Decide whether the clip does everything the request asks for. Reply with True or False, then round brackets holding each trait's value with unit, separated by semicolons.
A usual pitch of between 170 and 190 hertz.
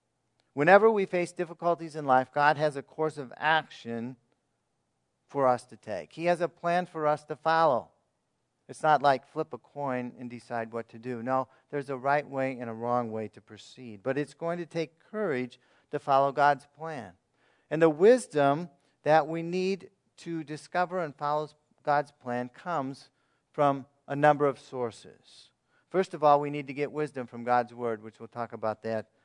False (145 Hz)